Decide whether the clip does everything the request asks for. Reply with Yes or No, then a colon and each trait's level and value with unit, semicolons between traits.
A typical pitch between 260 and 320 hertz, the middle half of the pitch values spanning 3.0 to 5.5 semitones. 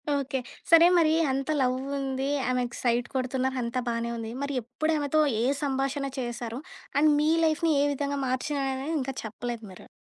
No: very high, 265 Hz; narrow, 2.6 semitones